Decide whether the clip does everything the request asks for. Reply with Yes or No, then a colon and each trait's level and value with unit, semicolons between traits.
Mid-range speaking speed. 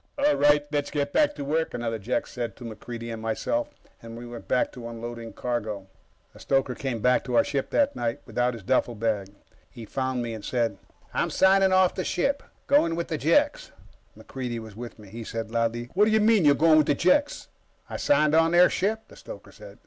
No: fast, 215 wpm